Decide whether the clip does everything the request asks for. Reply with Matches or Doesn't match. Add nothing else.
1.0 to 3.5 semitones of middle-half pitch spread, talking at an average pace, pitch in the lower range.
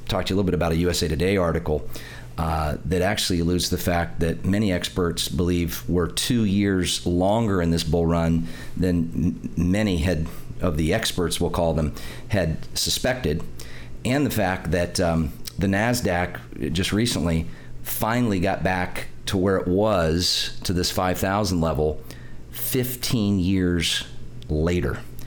Matches